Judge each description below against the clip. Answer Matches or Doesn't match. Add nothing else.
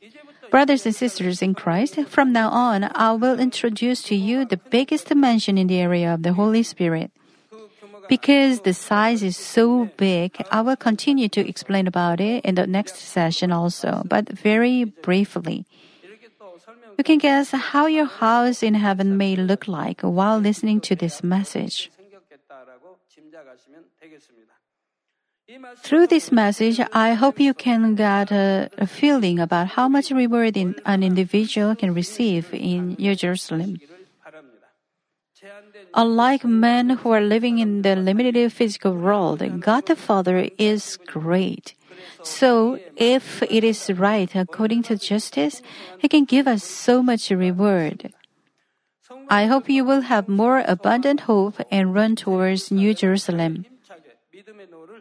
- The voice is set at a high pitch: Matches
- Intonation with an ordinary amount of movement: Matches